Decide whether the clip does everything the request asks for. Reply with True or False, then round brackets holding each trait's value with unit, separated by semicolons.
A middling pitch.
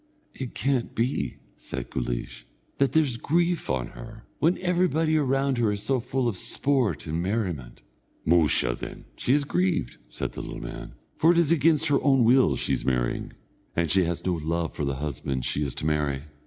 False (115 Hz)